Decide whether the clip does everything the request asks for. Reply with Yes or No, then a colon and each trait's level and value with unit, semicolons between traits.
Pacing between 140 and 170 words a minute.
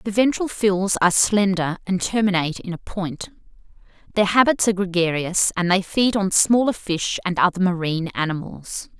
Yes: average, 160 wpm